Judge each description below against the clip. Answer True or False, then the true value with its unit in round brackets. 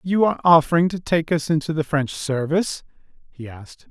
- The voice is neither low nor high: True (155 Hz)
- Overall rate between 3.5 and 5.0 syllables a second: False (5.8 syllables/s)